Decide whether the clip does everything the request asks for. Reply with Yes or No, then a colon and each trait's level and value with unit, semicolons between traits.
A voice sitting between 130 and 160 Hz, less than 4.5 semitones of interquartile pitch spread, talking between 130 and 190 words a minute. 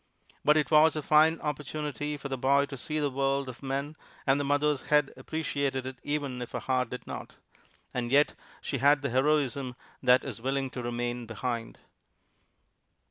Yes: medium, 140 Hz; narrow, 2.6 semitones; average, 180 wpm